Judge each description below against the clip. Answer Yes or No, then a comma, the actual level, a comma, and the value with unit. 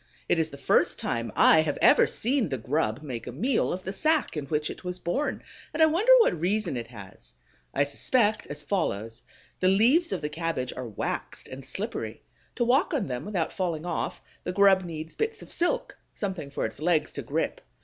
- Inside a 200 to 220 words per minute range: Yes, fast, 205 wpm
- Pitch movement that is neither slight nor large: No, wide, 7.8 semitones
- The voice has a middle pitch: Yes, medium, 170 Hz